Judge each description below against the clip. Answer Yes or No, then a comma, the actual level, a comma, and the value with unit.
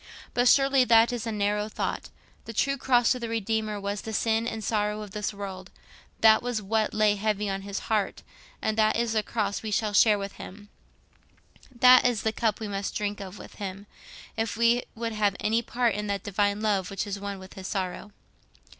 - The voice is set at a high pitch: Yes, high, 210 Hz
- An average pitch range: No, narrow, 2.0 semitones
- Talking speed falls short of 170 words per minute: No, average, 200 wpm